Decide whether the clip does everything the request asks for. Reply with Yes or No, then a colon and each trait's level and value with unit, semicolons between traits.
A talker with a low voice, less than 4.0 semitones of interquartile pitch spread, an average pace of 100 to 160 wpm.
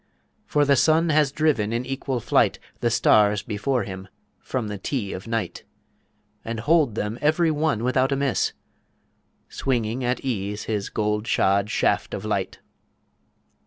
No: low, 120 Hz; average, 4.7 semitones; average, 150 wpm